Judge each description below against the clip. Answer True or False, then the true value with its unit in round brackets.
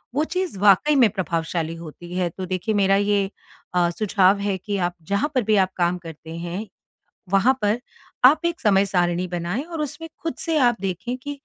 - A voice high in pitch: True (195 Hz)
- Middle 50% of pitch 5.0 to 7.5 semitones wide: True (5.5 semitones)